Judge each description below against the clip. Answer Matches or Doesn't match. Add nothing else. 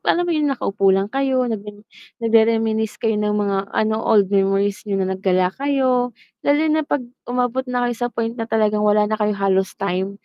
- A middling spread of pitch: Matches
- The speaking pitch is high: Matches